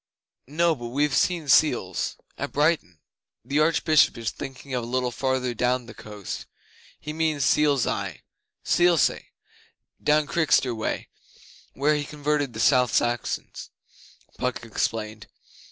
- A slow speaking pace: Yes, slow, 130 wpm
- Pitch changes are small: No, average, 4.0 semitones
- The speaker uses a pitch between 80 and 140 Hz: Yes, low, 135 Hz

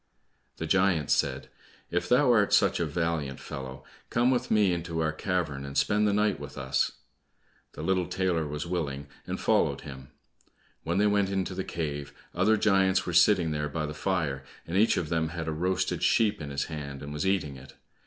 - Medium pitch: No, very low, 85 Hz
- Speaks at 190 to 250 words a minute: Yes, average, 195 wpm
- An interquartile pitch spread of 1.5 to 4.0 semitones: No, average, 4.7 semitones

